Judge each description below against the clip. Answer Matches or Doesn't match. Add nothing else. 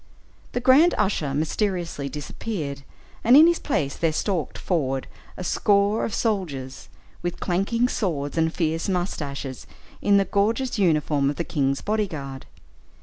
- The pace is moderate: Matches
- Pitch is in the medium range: Matches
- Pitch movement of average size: Doesn't match